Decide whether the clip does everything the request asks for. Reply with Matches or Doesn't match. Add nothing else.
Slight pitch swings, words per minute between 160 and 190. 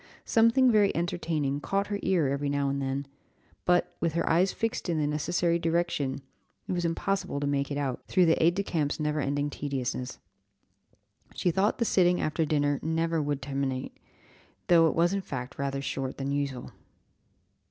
Doesn't match